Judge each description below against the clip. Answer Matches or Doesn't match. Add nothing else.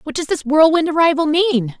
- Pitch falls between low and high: Doesn't match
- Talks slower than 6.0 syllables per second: Matches